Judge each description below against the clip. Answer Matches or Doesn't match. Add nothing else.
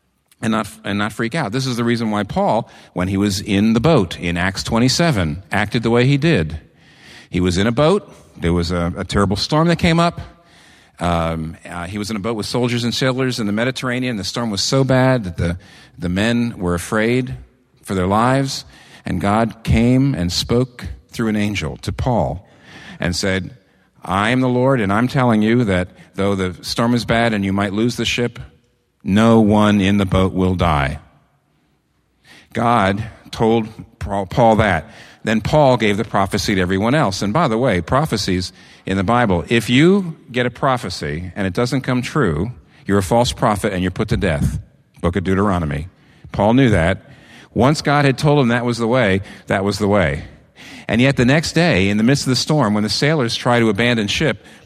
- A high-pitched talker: Doesn't match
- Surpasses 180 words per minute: Matches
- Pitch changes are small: Doesn't match